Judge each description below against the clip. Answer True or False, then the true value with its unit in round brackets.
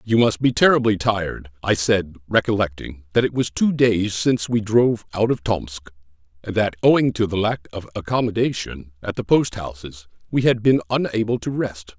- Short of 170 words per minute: False (185 wpm)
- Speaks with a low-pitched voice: True (105 Hz)